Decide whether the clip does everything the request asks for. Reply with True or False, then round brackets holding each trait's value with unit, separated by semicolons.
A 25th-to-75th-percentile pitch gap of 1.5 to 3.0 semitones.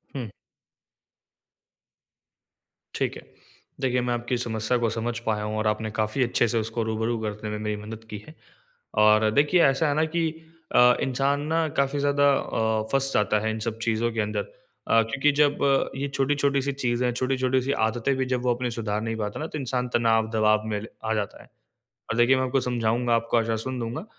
False (3.5 semitones)